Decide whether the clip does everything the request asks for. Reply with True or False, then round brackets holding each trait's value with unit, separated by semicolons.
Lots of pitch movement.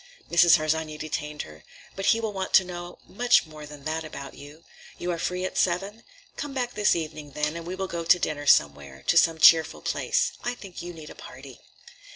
False (3.8 semitones)